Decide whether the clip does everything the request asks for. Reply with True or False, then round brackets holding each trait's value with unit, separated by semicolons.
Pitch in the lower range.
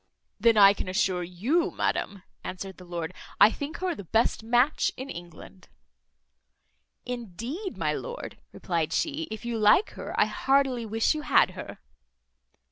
False (225 Hz)